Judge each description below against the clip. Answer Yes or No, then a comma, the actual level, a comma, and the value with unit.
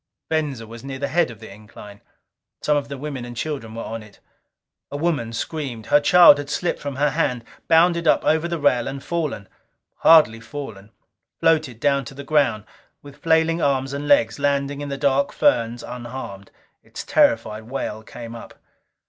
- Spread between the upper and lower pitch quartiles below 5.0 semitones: Yes, average, 4.4 semitones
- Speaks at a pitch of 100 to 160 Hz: Yes, medium, 140 Hz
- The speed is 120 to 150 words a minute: No, average, 180 wpm